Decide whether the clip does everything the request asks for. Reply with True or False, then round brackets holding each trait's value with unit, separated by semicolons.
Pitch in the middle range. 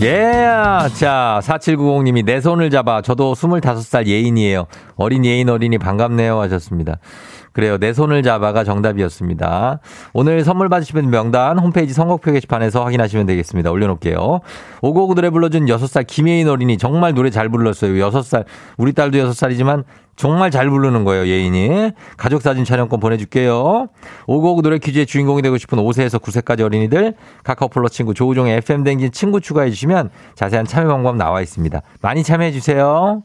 False (130 Hz)